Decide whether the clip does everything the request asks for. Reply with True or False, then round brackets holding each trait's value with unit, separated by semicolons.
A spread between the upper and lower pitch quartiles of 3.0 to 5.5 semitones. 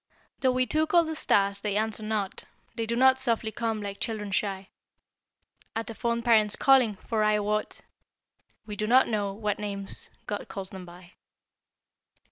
False (2.5 semitones)